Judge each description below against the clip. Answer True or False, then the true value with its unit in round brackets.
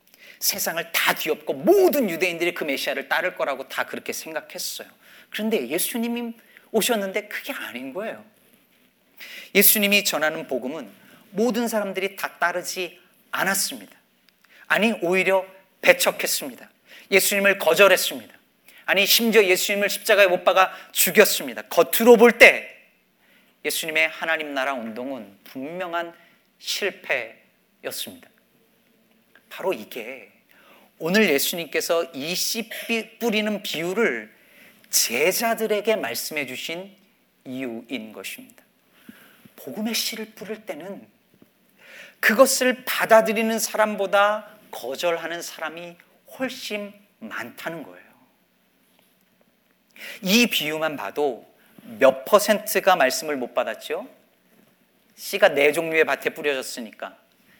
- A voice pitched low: False (200 Hz)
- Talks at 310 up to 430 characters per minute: False (260 characters per minute)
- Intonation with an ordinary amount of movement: True (4.4 semitones)